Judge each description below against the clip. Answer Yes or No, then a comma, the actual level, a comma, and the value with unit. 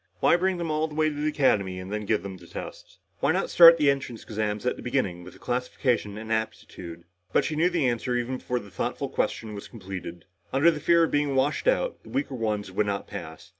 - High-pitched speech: No, low, 125 Hz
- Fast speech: Yes, fast, 235 wpm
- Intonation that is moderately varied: No, wide, 6.8 semitones